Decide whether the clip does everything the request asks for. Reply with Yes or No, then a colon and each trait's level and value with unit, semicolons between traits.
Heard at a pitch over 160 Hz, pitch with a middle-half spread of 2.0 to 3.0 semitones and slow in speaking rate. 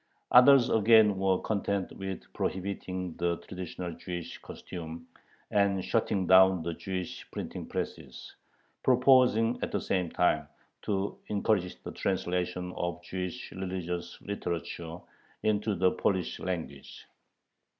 No: very low, 95 Hz; narrow, 2.6 semitones; slow, 115 wpm